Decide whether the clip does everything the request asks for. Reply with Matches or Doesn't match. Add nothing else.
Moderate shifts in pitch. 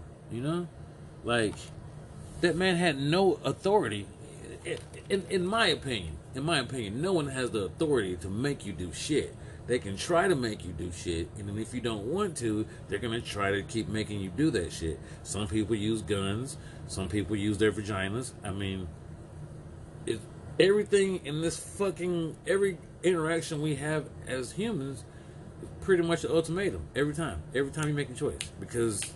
Doesn't match